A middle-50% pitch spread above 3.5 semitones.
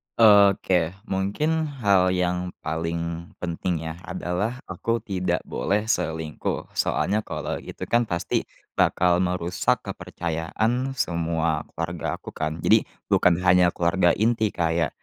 No: average, 3.2 semitones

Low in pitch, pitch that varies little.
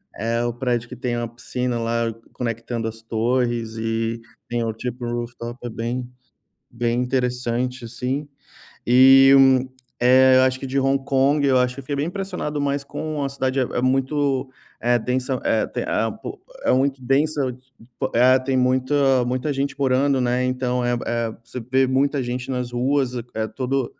Yes: low, 125 Hz; narrow, 2.1 semitones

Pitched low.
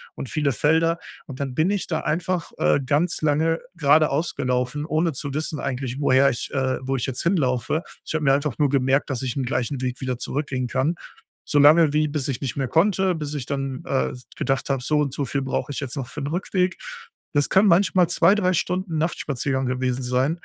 No: medium, 145 Hz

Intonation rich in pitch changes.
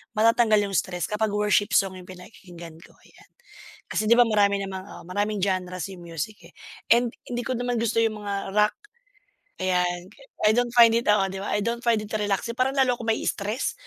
No: average, 3.5 semitones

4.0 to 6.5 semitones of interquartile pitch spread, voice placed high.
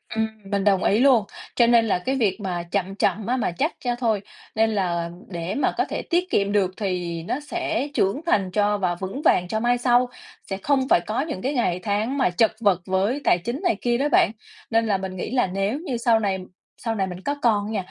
Yes: average, 4.5 semitones; high, 210 Hz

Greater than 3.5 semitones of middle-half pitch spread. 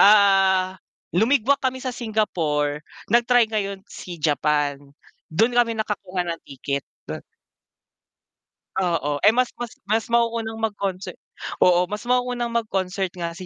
Yes: average, 4.7 semitones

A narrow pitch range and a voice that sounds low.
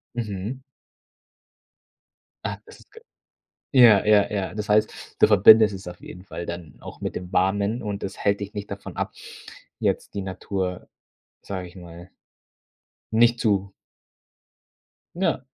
Yes: narrow, 2.3 semitones; low, 100 Hz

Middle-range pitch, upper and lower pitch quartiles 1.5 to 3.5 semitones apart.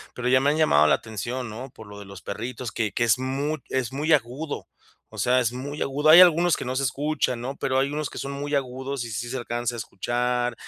No: low, 130 Hz; average, 2.9 semitones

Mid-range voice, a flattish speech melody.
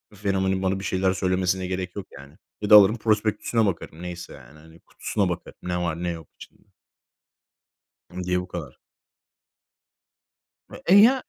No: very low, 95 Hz; narrow, 2.3 semitones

